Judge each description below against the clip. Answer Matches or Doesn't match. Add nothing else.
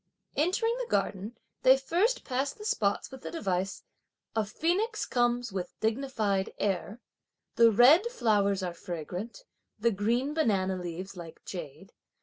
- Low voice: Doesn't match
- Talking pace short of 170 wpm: Matches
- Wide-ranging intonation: Matches